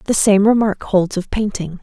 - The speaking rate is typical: Yes, average, 195 wpm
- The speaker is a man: No, female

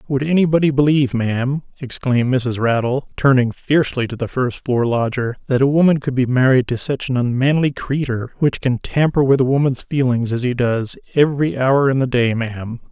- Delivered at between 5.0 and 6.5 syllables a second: Yes, 5.4 syllables/s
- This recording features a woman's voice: No, male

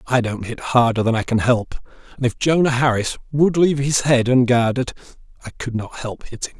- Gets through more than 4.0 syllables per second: Yes, 5.7 syllables/s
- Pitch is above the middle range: No, low, 125 Hz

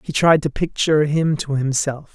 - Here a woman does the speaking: No, male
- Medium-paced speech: Yes, average, 195 wpm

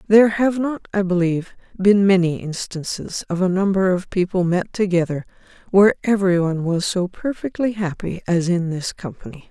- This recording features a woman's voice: Yes, female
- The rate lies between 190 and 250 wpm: No, average, 165 wpm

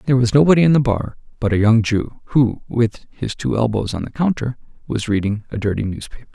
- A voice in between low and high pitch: No, low, 115 Hz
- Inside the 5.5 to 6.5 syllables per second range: Yes, 5.8 syllables/s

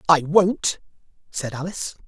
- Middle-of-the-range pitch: Yes, medium, 165 Hz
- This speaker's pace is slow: Yes, slow, 115 wpm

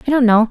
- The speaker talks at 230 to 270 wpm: No, fast, 355 wpm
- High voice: Yes, high, 240 Hz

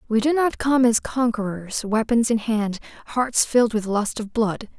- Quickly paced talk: No, average, 190 wpm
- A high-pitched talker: Yes, high, 230 Hz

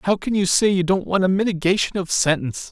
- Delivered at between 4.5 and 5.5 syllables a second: No, 6.0 syllables/s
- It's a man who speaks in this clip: Yes, male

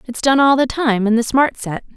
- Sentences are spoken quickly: Yes, fast, 275 wpm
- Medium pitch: No, very high, 250 Hz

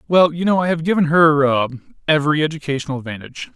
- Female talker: No, male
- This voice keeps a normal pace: Yes, average, 150 wpm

